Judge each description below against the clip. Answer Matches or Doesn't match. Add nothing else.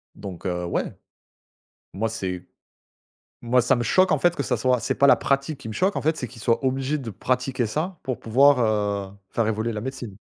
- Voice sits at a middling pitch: Doesn't match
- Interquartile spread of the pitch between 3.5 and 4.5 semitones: Matches